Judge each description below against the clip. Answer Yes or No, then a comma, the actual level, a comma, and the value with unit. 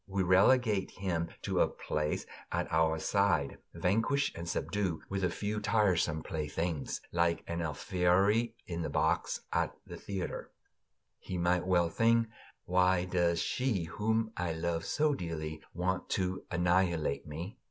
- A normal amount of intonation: Yes, average, 3.1 semitones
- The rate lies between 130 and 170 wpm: Yes, average, 140 wpm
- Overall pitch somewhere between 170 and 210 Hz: No, very low, 90 Hz